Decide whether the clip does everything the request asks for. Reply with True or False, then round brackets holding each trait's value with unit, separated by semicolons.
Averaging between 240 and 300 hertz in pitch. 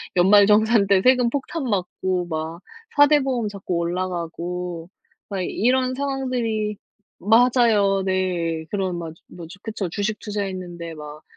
False (195 Hz)